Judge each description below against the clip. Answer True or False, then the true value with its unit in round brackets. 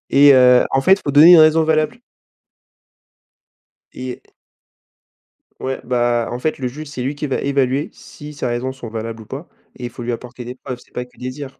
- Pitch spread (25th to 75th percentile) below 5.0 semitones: True (2.9 semitones)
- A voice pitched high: False (130 Hz)